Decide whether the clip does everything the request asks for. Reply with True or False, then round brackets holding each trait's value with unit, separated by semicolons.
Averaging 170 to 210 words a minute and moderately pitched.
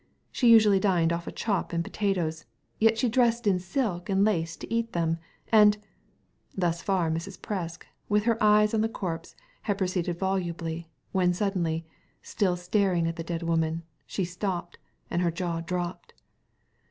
True (175 wpm; 180 Hz)